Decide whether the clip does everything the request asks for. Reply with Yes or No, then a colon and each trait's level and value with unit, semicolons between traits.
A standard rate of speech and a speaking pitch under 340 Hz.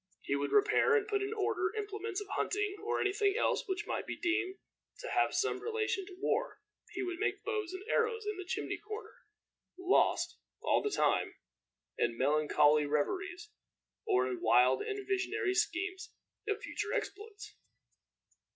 No: average, 160 wpm; very high, 400 Hz